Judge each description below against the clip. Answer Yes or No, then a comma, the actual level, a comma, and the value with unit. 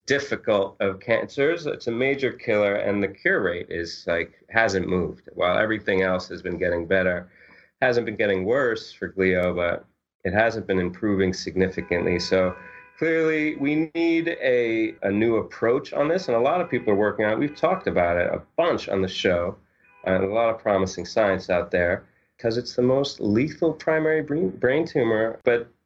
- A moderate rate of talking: Yes, average, 185 wpm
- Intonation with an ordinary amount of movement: No, wide, 5.8 semitones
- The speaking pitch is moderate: No, low, 105 Hz